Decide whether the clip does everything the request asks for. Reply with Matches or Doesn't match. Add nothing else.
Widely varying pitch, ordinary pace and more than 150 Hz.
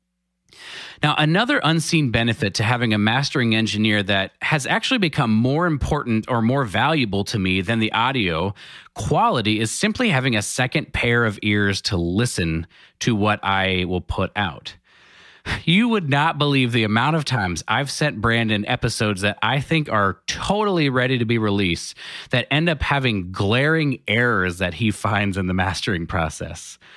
Doesn't match